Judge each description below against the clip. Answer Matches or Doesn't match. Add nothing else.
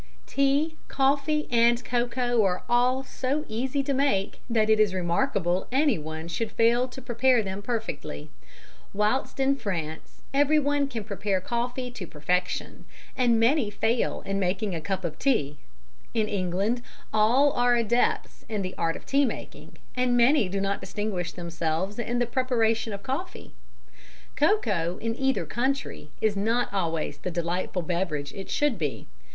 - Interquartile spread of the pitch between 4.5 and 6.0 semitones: Matches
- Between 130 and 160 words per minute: Matches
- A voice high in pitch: Matches